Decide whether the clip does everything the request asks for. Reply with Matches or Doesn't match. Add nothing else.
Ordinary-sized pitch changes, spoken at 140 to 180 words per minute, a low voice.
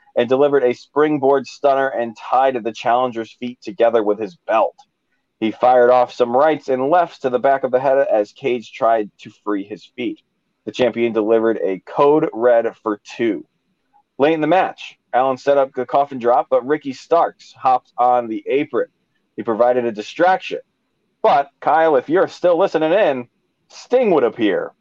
Matches